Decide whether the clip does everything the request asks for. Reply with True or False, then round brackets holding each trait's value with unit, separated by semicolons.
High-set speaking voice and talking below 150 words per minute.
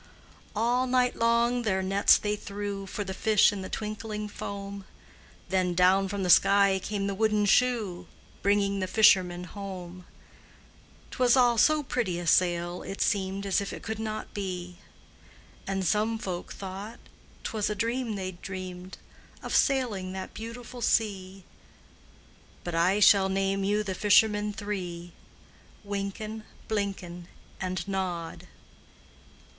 True (200 Hz; 140 wpm)